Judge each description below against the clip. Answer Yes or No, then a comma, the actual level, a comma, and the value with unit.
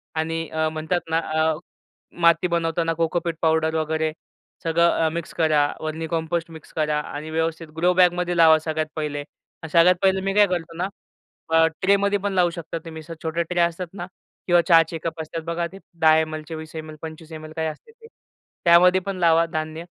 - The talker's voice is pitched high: No, medium, 165 Hz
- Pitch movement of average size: No, narrow, 1.6 semitones